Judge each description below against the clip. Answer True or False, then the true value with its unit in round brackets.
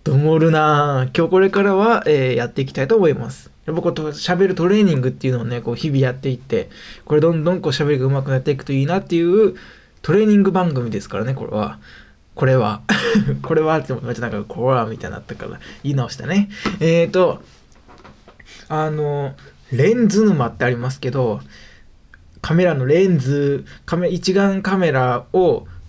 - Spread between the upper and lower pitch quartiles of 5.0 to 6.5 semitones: True (5.4 semitones)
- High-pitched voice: False (145 Hz)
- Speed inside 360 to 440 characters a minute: True (380 characters per minute)